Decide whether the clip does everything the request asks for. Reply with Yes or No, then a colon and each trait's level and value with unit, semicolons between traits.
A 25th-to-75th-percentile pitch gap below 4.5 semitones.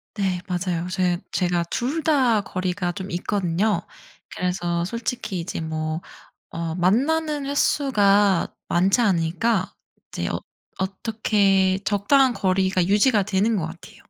Yes: average, 3.8 semitones